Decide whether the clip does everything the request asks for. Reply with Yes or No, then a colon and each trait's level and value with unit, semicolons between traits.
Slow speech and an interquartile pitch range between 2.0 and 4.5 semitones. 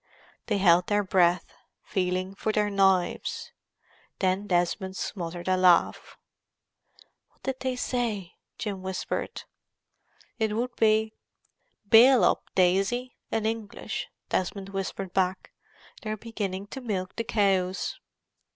Yes: slow, 115 wpm; average, 2.9 semitones